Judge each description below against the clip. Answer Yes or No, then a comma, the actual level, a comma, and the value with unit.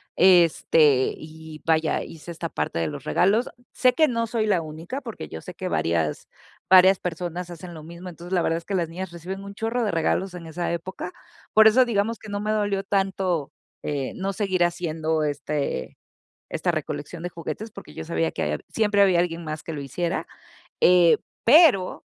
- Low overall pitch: No, medium, 175 Hz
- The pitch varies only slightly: No, average, 3.9 semitones